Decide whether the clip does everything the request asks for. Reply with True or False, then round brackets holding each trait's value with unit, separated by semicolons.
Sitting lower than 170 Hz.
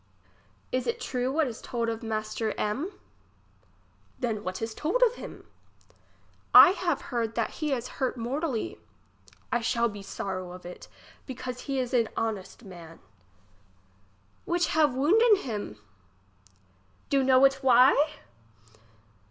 False (245 Hz)